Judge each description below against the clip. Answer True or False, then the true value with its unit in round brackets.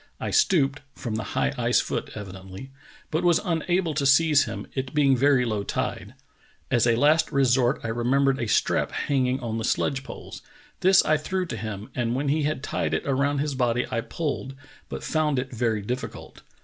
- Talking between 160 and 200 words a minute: True (190 wpm)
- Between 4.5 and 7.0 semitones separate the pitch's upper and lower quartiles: False (4.0 semitones)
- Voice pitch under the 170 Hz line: True (135 Hz)